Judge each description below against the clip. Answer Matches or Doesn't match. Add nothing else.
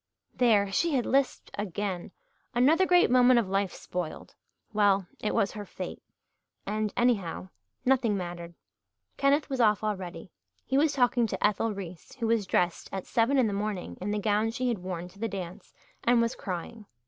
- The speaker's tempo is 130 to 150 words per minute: Doesn't match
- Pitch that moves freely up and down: Doesn't match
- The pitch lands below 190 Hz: Doesn't match